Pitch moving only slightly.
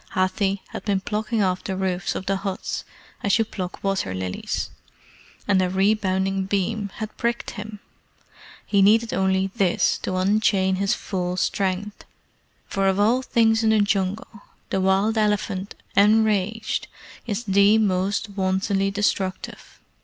Yes: narrow, 2.0 semitones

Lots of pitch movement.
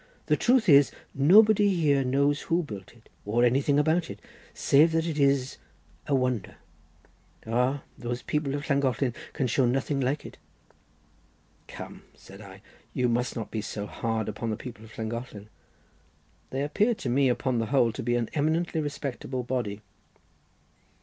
No: average, 3.7 semitones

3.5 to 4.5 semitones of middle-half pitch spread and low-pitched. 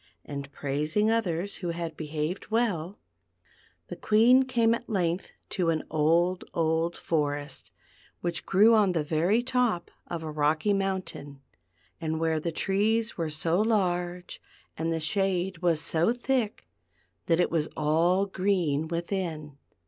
No: average, 4.1 semitones; medium, 175 Hz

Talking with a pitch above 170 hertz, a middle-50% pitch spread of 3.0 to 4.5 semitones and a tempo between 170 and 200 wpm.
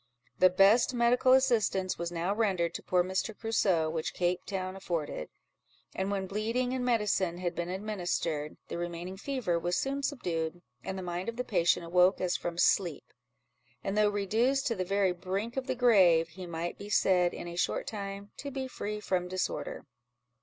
Yes: high, 190 Hz; average, 3.9 semitones; average, 180 wpm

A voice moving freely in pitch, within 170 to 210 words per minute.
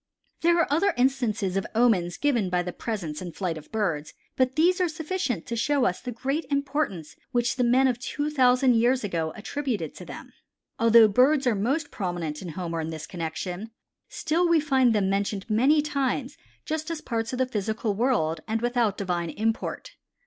Yes: wide, 6.3 semitones; average, 185 wpm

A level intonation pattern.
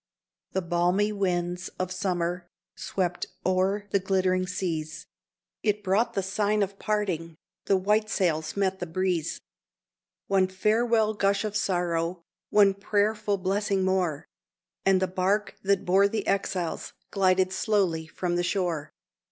Yes: narrow, 2.1 semitones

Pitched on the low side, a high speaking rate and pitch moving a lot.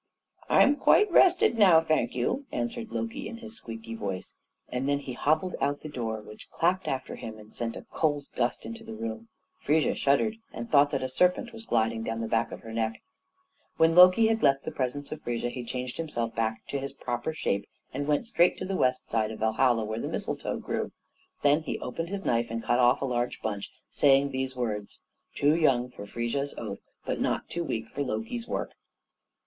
Yes: low, 130 Hz; fast, 210 wpm; wide, 6.0 semitones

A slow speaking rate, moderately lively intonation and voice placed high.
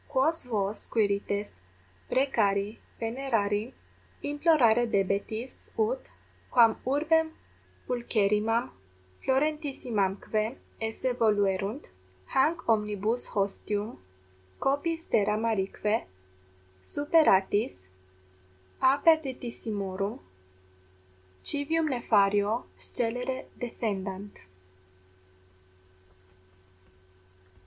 Yes: slow, 60 wpm; average, 4.7 semitones; high, 225 Hz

